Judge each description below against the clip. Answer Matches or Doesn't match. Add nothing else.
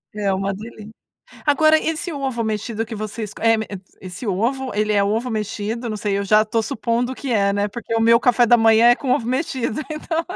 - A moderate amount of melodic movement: Matches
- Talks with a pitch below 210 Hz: Doesn't match